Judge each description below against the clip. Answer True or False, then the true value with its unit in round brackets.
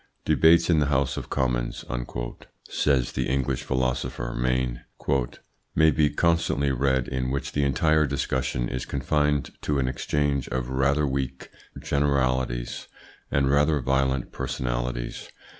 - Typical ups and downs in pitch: False (2.2 semitones)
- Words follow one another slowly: True (125 wpm)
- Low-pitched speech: True (65 Hz)